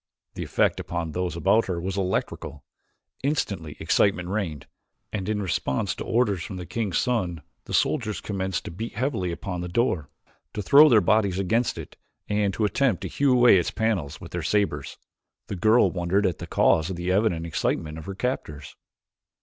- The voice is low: Yes, very low, 95 Hz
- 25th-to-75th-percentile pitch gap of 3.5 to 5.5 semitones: Yes, average, 4.1 semitones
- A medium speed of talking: Yes, average, 180 wpm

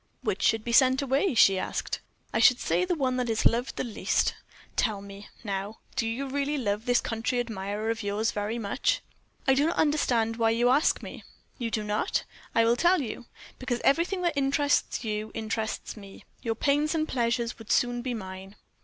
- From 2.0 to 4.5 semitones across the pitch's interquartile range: Yes, average, 3.9 semitones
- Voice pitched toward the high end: Yes, high, 235 Hz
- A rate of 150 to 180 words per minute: No, average, 195 wpm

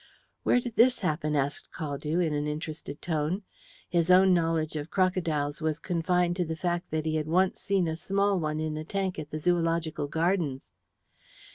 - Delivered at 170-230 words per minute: Yes, average, 180 wpm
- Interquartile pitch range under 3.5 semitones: Yes, average, 2.9 semitones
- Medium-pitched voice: Yes, medium, 165 Hz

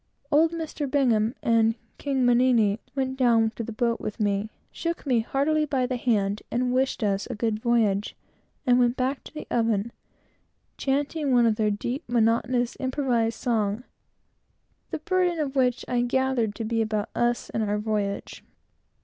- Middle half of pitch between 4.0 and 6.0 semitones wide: No, average, 3.2 semitones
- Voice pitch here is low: No, high, 240 Hz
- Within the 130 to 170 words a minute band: Yes, average, 160 wpm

